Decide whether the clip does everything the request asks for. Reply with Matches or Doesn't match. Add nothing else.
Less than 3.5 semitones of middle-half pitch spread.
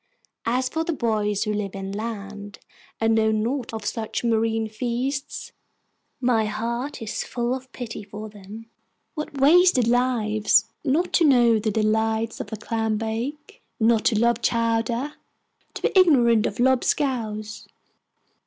Matches